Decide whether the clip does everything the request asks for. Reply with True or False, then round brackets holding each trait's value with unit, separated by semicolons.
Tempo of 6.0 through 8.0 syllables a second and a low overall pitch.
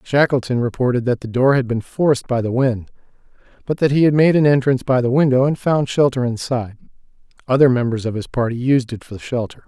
True (6.1 syllables/s; 130 Hz)